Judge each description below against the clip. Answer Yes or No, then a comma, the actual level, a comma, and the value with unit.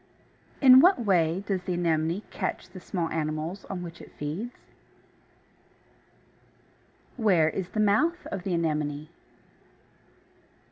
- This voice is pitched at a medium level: Yes, medium, 180 Hz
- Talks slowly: Yes, slow, 130 wpm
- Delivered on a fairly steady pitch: No, average, 4.2 semitones